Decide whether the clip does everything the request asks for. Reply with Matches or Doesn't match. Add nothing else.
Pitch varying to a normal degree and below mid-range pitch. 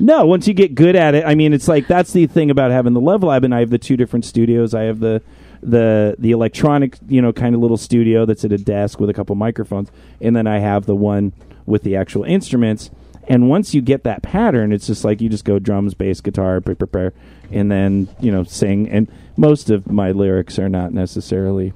Matches